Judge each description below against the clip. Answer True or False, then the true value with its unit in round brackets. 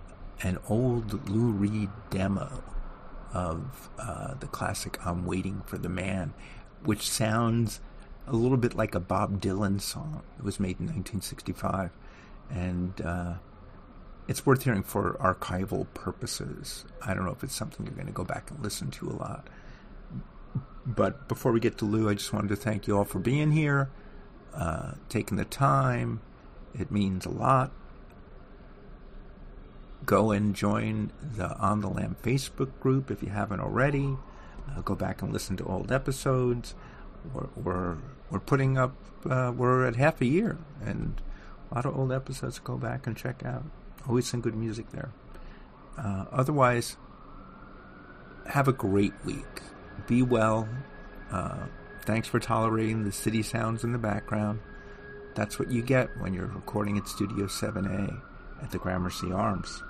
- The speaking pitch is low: True (110 Hz)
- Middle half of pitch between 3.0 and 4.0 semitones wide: False (4.5 semitones)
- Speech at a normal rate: True (155 wpm)